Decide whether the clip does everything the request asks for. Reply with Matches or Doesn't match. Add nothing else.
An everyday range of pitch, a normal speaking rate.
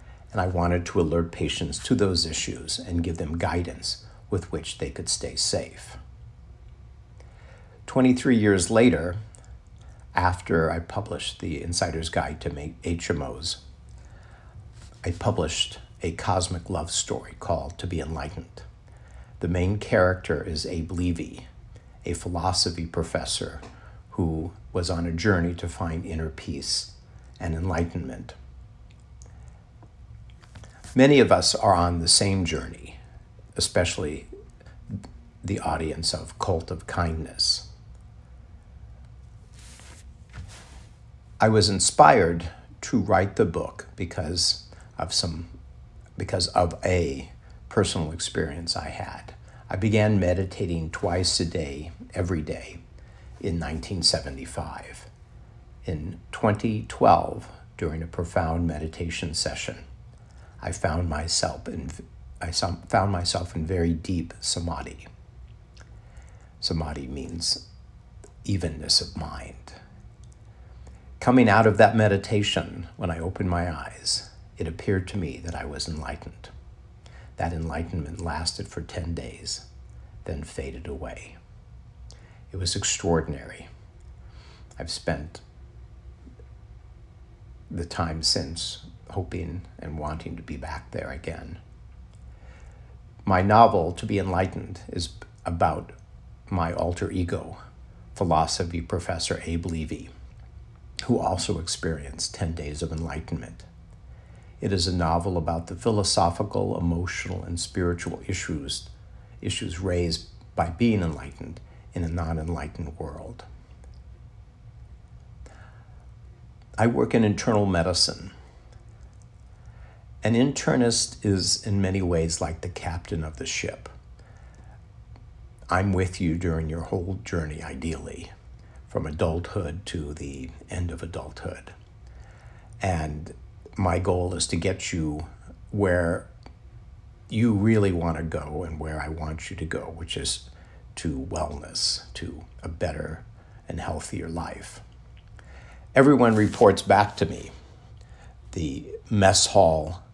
Doesn't match